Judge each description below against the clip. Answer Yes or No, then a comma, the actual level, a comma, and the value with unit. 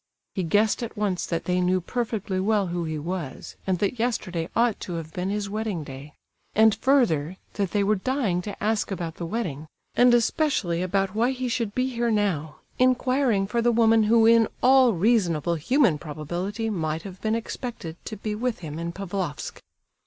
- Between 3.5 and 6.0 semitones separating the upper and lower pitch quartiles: Yes, average, 5.0 semitones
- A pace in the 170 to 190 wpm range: Yes, average, 185 wpm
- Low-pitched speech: No, high, 200 Hz